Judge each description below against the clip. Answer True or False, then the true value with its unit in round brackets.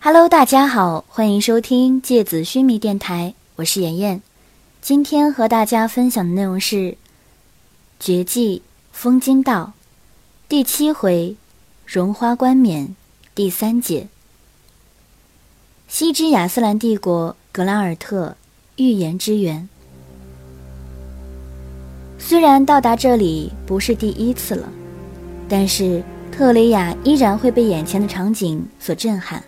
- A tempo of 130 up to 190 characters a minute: True (180 characters per minute)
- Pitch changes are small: False (5.8 semitones)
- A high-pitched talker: True (205 Hz)